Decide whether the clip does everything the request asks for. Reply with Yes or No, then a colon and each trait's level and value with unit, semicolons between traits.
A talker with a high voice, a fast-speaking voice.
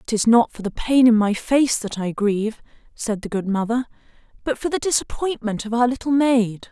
Yes: high, 230 Hz; fast, 215 wpm